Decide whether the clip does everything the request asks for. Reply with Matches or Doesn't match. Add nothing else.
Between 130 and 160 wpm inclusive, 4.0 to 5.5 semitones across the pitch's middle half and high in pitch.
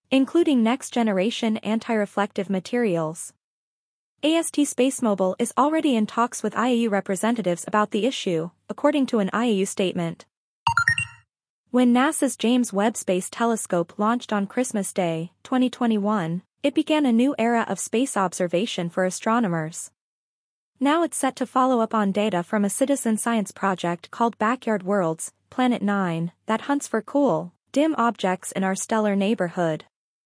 Matches